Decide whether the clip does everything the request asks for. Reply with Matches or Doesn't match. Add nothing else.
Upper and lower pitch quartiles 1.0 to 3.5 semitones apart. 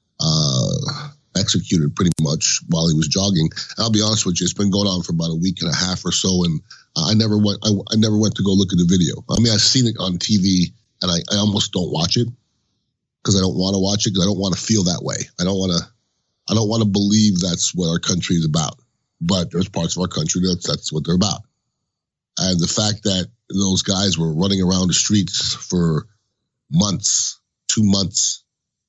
Matches